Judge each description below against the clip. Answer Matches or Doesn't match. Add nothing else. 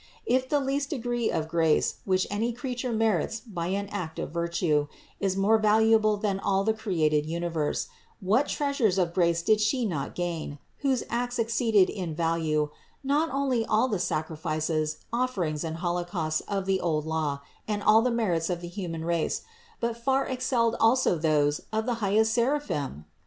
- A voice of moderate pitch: Doesn't match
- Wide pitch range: Matches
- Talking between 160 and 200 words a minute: Matches